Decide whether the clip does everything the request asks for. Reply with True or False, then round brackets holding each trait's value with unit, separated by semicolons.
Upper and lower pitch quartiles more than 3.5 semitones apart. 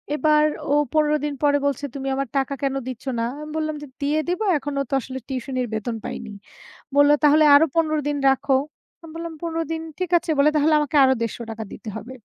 False (2.7 semitones)